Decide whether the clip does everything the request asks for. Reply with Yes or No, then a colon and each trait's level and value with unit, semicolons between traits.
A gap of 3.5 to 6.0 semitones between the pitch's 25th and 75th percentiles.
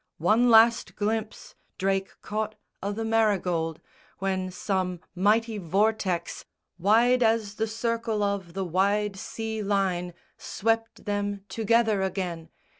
No: average, 2.9 semitones